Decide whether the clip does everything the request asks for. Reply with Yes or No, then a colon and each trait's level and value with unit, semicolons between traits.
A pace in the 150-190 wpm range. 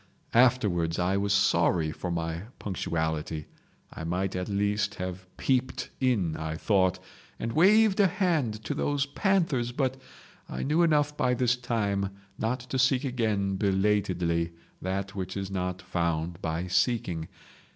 No: average, 140 wpm